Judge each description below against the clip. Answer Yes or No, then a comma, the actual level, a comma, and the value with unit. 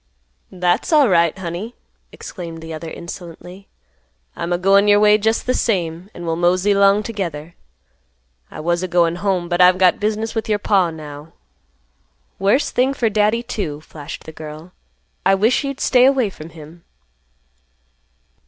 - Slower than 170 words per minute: Yes, average, 155 wpm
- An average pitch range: Yes, average, 3.9 semitones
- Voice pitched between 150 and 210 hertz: Yes, medium, 185 Hz